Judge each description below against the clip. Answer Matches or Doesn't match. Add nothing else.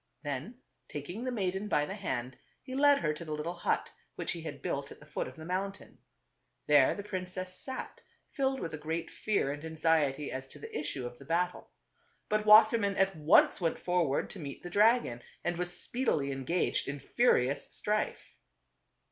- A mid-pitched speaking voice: Matches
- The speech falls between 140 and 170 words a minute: Doesn't match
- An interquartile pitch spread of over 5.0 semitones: Matches